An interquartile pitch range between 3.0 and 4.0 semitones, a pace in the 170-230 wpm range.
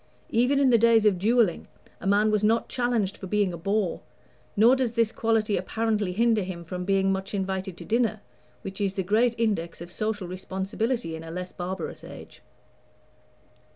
Yes: average, 3.3 semitones; average, 180 wpm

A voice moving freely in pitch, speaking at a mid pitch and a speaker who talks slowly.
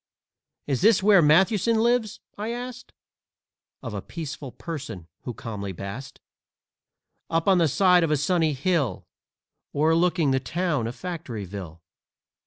Yes: wide, 6.2 semitones; medium, 160 Hz; slow, 130 wpm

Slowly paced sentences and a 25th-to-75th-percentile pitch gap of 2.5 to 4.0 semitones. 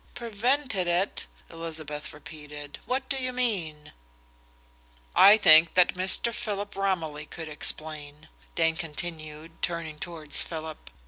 No: slow, 115 wpm; average, 4.4 semitones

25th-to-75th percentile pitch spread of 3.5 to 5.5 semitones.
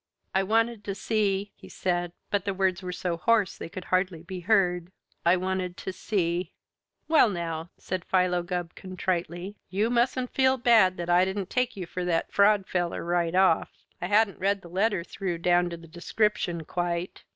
No: narrow, 2.6 semitones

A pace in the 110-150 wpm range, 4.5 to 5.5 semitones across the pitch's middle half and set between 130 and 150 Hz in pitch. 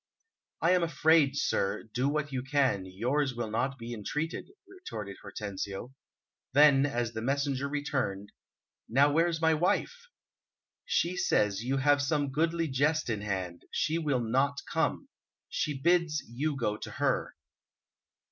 Yes: average, 140 wpm; average, 4.9 semitones; medium, 140 Hz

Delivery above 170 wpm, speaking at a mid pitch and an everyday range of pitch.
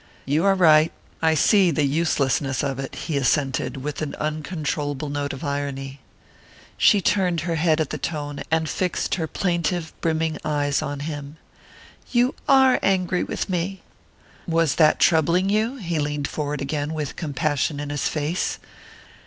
No: average, 155 wpm; medium, 155 Hz; average, 3.0 semitones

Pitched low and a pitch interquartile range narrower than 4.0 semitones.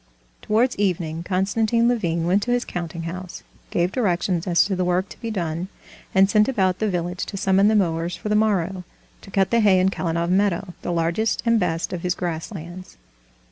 No: medium, 185 Hz; average, 3.2 semitones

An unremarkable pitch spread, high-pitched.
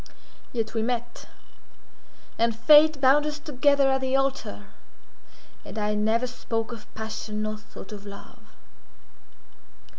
Yes: average, 4.1 semitones; high, 235 Hz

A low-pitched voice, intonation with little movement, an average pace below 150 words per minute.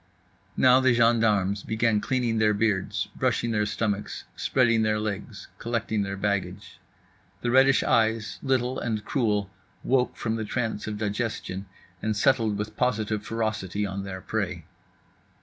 Yes: low, 110 Hz; narrow, 2.3 semitones; average, 140 wpm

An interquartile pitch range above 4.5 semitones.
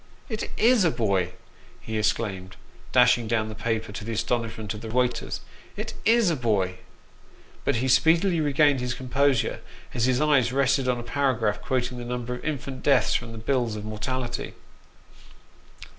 No: average, 3.7 semitones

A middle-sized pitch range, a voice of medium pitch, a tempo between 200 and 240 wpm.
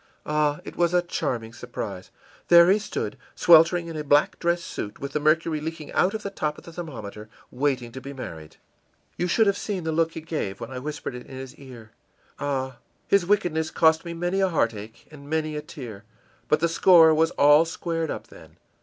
Yes: average, 4.4 semitones; medium, 155 Hz; fast, 205 wpm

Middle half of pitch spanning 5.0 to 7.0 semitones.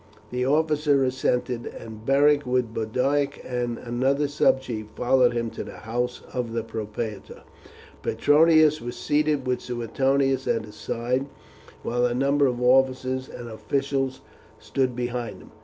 No: narrow, 2.5 semitones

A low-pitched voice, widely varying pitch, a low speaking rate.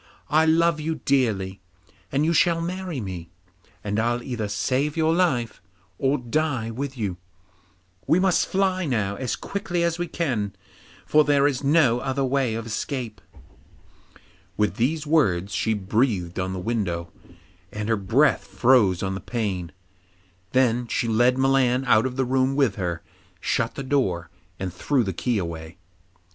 No: low, 125 Hz; wide, 6.0 semitones; average, 155 wpm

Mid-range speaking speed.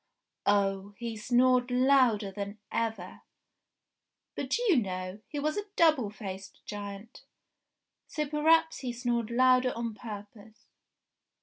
No: slow, 115 wpm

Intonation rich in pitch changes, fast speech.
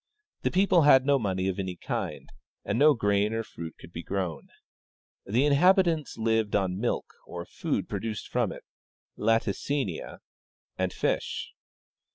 No: wide, 6.9 semitones; average, 145 wpm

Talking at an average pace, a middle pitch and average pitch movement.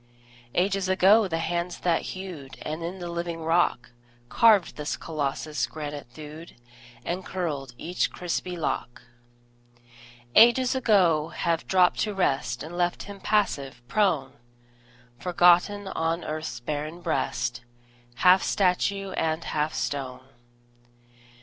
No: slow, 120 wpm; medium, 170 Hz; average, 3.8 semitones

